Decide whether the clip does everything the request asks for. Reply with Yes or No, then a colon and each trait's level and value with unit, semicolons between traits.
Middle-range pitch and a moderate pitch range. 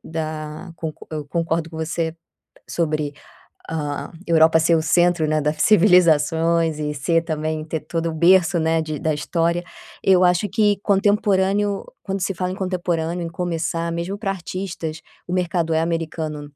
No: medium, 165 Hz; narrow, 2.3 semitones